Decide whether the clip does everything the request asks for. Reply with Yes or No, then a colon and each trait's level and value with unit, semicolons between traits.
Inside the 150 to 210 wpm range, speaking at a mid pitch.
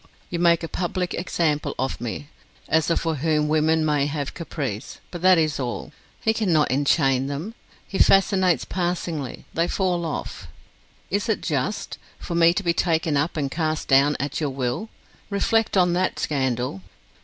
Yes: average, 170 wpm; medium, 160 Hz